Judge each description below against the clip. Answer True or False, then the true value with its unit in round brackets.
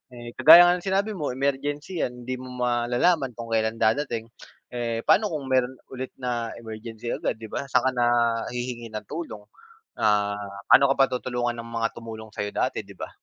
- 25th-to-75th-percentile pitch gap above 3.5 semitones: False (3.0 semitones)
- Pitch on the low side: True (120 Hz)